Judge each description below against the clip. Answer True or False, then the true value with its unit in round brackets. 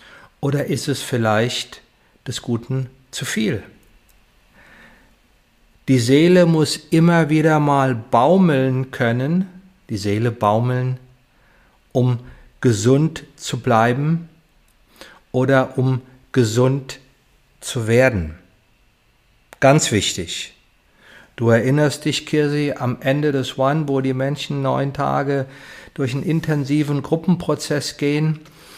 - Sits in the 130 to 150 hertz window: True (135 Hz)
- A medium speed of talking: False (100 wpm)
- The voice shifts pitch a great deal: False (3.3 semitones)